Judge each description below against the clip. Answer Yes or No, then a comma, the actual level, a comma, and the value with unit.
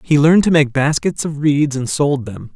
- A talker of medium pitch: Yes, medium, 145 Hz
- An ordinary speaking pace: No, fast, 235 wpm